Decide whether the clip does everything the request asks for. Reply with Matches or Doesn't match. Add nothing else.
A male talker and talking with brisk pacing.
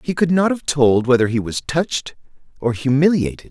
Doesn't match